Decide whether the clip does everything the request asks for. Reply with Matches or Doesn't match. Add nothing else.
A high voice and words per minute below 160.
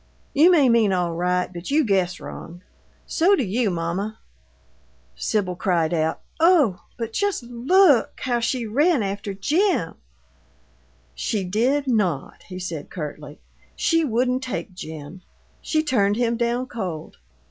Matches